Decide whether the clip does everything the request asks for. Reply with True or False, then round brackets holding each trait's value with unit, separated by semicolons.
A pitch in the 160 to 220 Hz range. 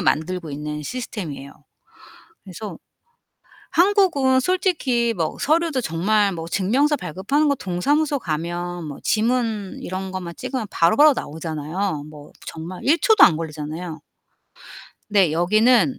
True (190 Hz)